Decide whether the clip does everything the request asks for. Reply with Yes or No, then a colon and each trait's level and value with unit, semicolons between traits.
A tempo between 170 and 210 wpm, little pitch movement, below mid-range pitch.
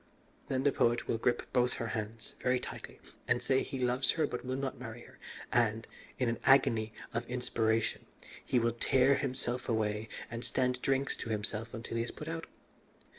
Yes: average, 185 wpm; narrow, 2.3 semitones; low, 120 Hz